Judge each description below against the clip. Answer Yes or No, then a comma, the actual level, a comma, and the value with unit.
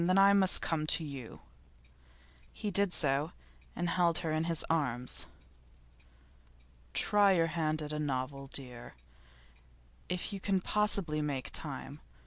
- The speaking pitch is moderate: Yes, medium, 160 Hz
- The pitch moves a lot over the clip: No, average, 4.3 semitones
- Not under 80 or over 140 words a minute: Yes, slow, 135 wpm